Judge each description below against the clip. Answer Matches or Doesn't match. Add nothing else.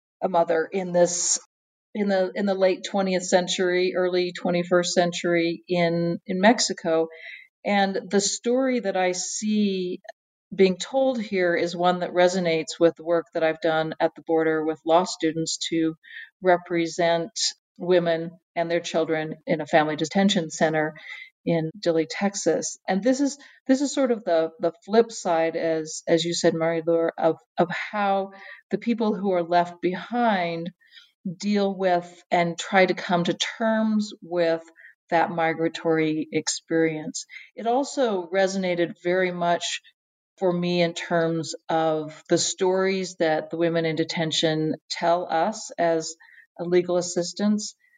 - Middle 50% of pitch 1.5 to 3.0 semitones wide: Matches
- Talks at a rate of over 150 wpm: Doesn't match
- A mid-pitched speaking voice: Matches